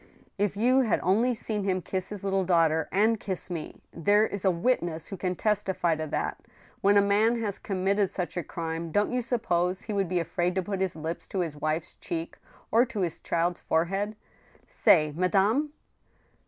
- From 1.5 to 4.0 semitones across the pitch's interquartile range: Yes, average, 3.3 semitones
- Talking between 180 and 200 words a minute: Yes, average, 195 wpm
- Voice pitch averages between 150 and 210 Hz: Yes, high, 190 Hz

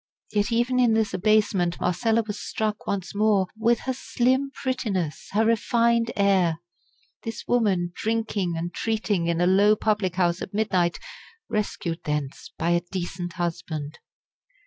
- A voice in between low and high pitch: No, high, 205 Hz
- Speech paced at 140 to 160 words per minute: Yes, average, 145 wpm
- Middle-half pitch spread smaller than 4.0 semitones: No, average, 4.3 semitones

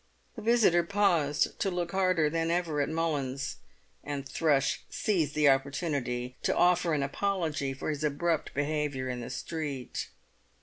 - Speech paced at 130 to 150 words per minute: Yes, average, 145 wpm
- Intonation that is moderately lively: Yes, average, 3.6 semitones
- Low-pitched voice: No, medium, 150 Hz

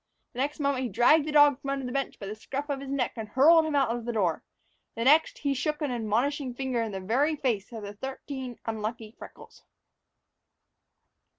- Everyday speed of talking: No, fast, 210 wpm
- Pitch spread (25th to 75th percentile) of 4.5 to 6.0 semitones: No, average, 4.0 semitones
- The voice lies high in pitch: Yes, very high, 260 Hz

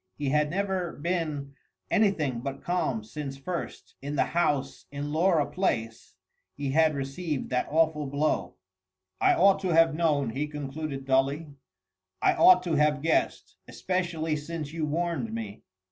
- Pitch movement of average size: Yes, average, 3.4 semitones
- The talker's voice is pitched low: No, medium, 150 Hz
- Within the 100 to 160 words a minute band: Yes, average, 145 wpm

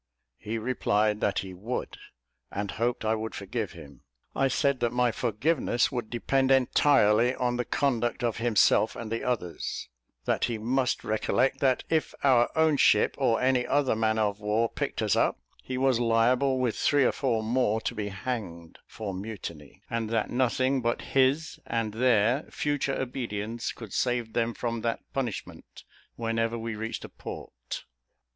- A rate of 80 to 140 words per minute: No, average, 165 wpm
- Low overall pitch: Yes, low, 115 Hz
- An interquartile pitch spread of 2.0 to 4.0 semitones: Yes, average, 2.9 semitones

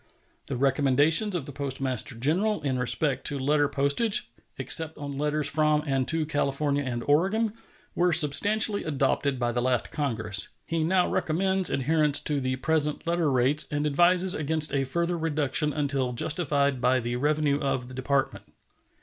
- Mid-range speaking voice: Yes, medium, 145 Hz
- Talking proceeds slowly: No, average, 160 wpm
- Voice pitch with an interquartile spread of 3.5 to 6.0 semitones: No, average, 3.1 semitones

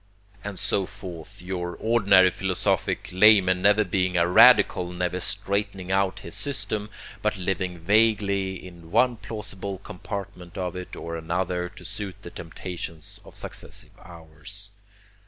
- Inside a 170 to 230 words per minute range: No, slow, 135 wpm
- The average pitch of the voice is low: Yes, very low, 95 Hz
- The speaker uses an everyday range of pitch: No, narrow, 2.3 semitones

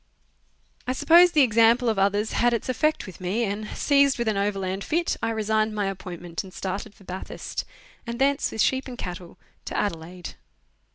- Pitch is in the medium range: No, high, 215 Hz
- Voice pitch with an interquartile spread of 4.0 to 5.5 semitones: Yes, average, 4.3 semitones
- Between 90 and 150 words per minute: No, average, 180 wpm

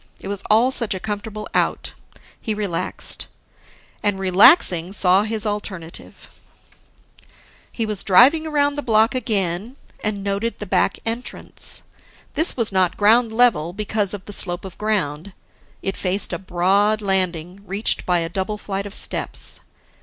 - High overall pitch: Yes, high, 205 Hz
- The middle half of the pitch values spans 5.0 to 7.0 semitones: No, average, 2.9 semitones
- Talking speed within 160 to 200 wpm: No, average, 145 wpm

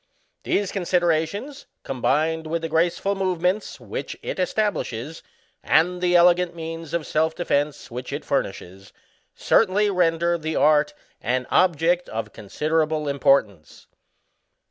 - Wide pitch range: No, average, 3.4 semitones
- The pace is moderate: No, slow, 120 wpm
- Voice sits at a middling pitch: Yes, medium, 165 Hz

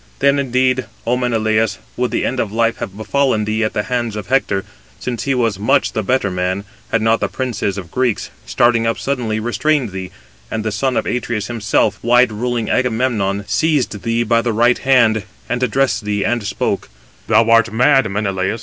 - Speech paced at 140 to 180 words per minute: No, average, 195 wpm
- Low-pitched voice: Yes, low, 115 Hz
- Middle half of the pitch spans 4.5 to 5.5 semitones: No, average, 2.9 semitones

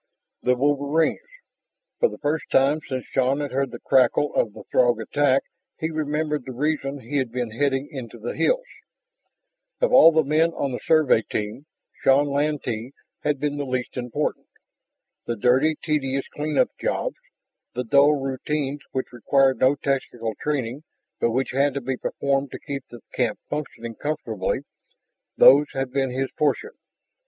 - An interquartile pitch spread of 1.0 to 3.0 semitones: Yes, average, 2.7 semitones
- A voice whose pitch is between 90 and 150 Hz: Yes, low, 135 Hz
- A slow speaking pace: No, average, 160 wpm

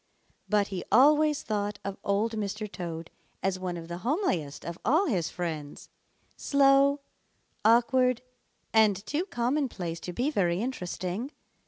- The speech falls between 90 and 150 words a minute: Yes, slow, 135 wpm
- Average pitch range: No, wide, 6.6 semitones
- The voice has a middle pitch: No, high, 210 Hz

